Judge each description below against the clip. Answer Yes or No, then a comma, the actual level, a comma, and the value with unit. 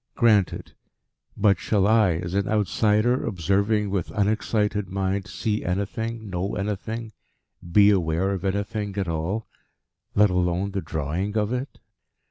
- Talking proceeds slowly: Yes, slow, 130 wpm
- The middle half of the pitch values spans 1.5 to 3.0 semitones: Yes, narrow, 2.4 semitones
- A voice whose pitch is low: Yes, low, 100 Hz